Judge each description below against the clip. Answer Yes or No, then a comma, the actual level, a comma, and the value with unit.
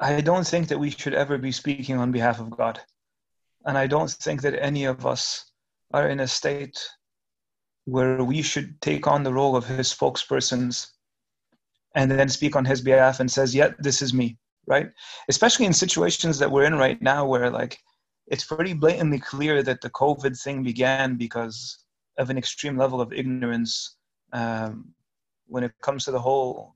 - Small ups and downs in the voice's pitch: Yes, narrow, 2.1 semitones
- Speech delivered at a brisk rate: No, average, 180 wpm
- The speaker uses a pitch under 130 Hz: No, low, 135 Hz